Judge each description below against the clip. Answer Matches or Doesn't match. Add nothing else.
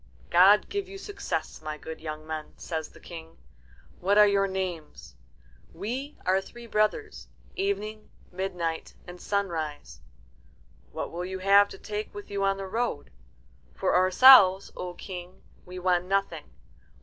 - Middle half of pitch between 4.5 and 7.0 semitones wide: Doesn't match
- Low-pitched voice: Doesn't match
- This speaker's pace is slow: Doesn't match